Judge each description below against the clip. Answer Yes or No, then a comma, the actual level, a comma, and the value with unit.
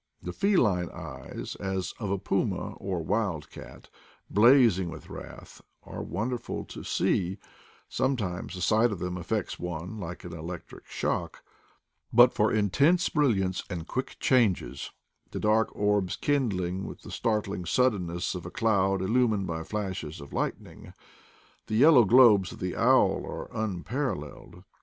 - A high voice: No, low, 100 Hz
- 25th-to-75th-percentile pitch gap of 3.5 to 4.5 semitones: Yes, average, 4.2 semitones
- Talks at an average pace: Yes, average, 145 wpm